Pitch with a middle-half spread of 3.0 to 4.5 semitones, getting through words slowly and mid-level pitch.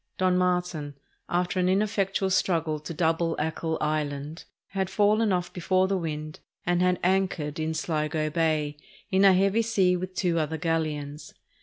No: average, 3.3 semitones; average, 155 wpm; medium, 175 Hz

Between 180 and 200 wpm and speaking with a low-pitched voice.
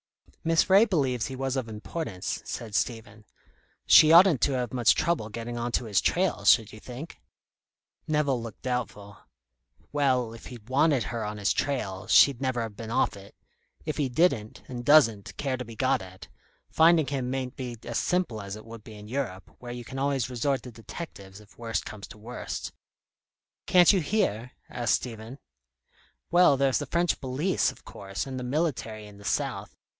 Yes: average, 185 wpm; low, 125 Hz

